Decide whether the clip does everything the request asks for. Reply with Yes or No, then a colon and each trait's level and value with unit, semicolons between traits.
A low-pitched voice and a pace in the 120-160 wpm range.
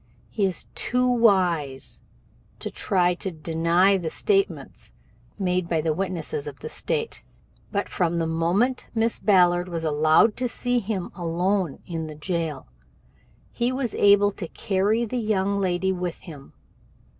No: medium, 185 Hz; average, 150 wpm